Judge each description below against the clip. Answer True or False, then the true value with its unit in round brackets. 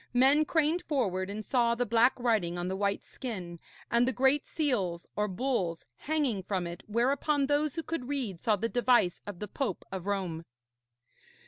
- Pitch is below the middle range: False (235 Hz)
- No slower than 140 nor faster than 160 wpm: False (180 wpm)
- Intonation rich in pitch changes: True (6.1 semitones)